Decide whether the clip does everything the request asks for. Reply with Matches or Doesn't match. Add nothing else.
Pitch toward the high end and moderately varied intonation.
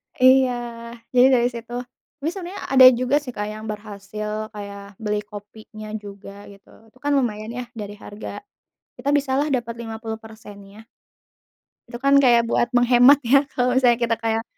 Matches